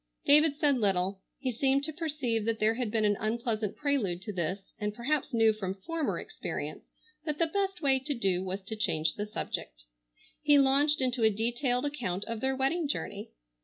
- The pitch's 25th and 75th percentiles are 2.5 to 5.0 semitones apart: No, wide, 5.5 semitones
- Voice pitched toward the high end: Yes, high, 235 Hz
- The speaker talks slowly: No, average, 190 wpm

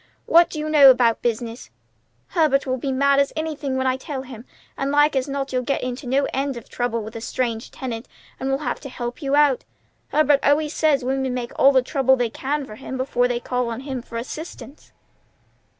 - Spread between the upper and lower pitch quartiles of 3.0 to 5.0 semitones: No, narrow, 2.4 semitones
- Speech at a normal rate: No, fast, 215 wpm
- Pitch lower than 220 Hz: No, very high, 265 Hz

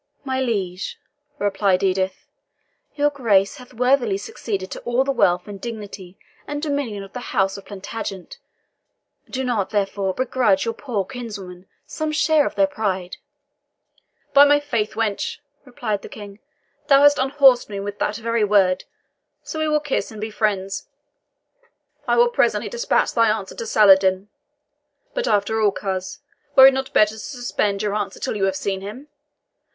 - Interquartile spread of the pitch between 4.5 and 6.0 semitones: Yes, average, 5.1 semitones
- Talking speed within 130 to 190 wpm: Yes, average, 165 wpm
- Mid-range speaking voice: No, high, 215 Hz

